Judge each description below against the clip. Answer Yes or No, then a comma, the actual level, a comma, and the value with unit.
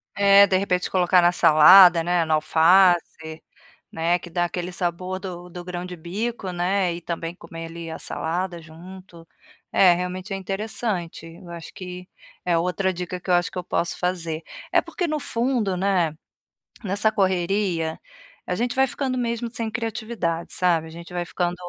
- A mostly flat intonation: Yes, narrow, 2.3 semitones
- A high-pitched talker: No, medium, 180 Hz